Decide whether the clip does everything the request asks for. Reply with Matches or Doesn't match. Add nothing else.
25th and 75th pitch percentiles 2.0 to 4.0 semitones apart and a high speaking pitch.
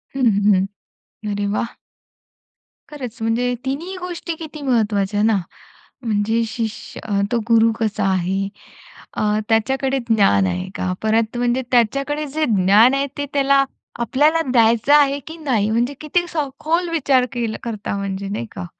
Doesn't match